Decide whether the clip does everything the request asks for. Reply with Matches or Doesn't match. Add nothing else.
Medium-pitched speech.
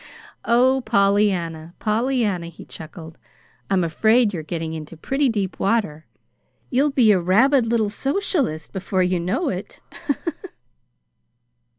Doesn't match